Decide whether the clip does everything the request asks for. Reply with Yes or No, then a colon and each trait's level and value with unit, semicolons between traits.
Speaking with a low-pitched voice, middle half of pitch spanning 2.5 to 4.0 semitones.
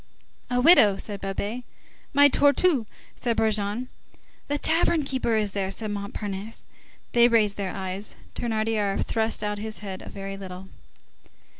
No: high, 215 Hz; average, 3.3 semitones